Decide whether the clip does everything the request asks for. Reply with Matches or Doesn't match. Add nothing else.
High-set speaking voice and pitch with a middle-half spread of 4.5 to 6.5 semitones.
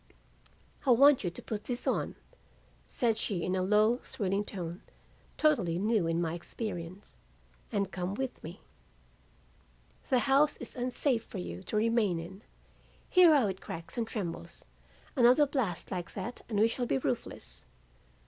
Matches